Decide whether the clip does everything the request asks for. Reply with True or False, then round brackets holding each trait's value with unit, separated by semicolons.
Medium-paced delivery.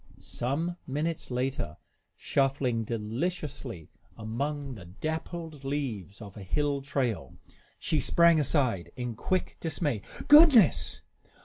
False (105 wpm)